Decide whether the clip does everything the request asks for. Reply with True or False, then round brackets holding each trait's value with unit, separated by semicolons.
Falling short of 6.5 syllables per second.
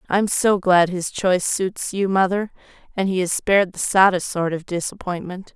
True (4.9 syllables/s)